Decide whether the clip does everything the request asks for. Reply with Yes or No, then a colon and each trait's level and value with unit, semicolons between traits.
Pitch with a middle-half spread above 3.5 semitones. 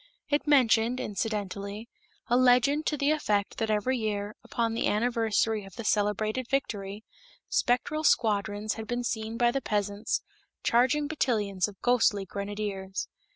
No: average, 3.1 semitones